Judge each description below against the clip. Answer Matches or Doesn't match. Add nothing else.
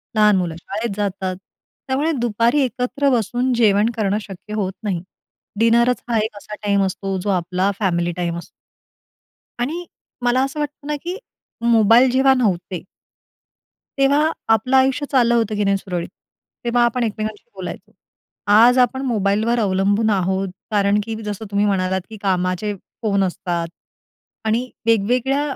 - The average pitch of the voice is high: Matches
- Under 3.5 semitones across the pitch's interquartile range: Doesn't match